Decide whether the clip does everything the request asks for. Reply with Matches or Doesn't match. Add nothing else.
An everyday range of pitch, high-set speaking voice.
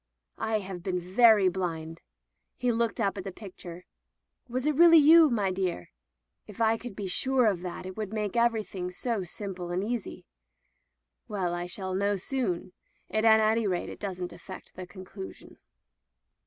Matches